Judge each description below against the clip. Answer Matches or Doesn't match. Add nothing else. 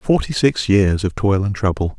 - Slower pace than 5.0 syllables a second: Matches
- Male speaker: Matches